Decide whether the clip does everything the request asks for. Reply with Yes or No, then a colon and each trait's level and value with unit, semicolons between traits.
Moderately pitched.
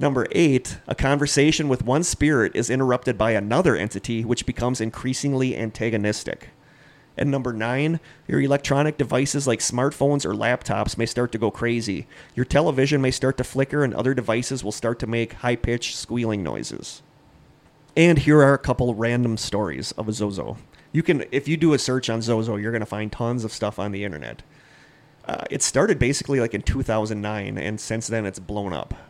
No: low, 120 Hz